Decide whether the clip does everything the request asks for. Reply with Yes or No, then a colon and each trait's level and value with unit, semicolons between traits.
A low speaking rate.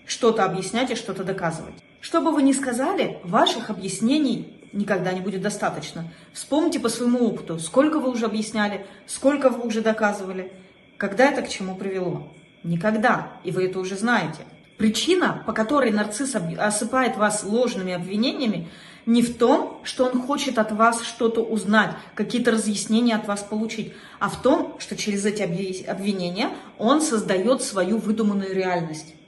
No: average, 150 wpm